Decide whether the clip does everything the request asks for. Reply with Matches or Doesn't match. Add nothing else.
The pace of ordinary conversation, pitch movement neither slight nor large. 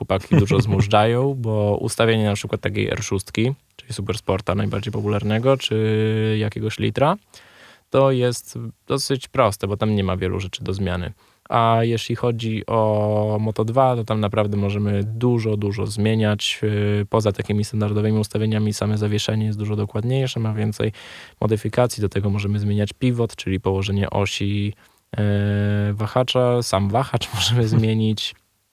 Doesn't match